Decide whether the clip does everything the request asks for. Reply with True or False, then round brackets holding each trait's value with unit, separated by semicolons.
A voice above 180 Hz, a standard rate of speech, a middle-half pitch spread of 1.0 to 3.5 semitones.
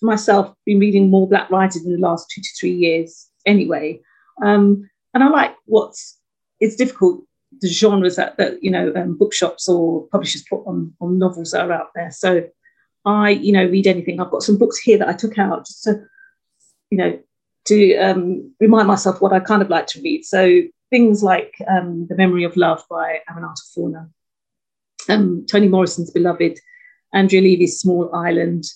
True (190 Hz; 185 wpm; 3.2 semitones)